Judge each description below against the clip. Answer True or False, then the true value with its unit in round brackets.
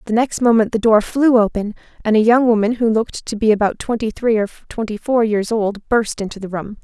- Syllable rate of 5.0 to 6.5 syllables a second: True (5.5 syllables/s)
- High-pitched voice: True (220 Hz)